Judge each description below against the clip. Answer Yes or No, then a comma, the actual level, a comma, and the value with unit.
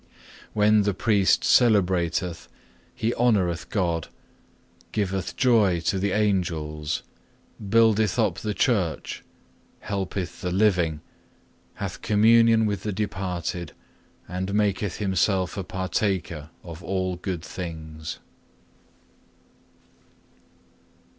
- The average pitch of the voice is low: Yes, very low, 95 Hz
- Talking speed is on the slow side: Yes, slow, 95 wpm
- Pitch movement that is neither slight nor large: Yes, average, 3.3 semitones